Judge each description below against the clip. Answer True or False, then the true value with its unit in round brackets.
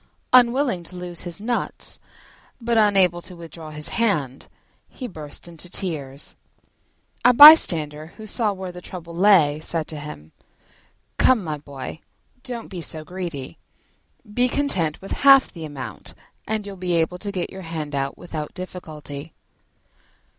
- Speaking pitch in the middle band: True (175 Hz)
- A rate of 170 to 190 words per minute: False (145 wpm)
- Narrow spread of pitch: False (5.0 semitones)